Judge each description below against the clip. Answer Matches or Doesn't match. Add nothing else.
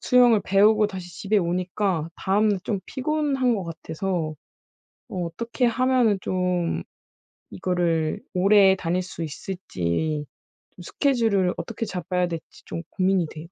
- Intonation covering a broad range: Doesn't match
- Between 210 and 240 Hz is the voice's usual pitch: Doesn't match